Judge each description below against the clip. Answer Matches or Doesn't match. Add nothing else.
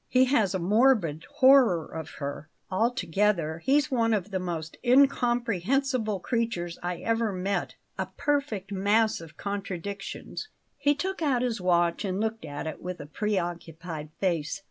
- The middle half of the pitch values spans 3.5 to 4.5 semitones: Doesn't match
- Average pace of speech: Matches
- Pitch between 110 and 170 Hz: Doesn't match